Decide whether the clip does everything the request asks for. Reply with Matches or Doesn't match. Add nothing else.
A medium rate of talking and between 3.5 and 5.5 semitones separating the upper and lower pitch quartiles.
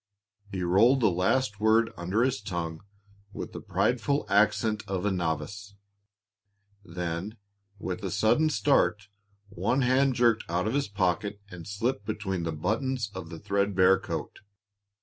Matches